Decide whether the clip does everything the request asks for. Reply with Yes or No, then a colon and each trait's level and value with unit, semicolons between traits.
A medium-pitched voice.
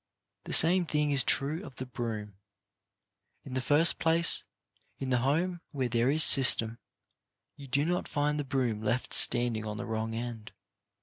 No: low, 130 Hz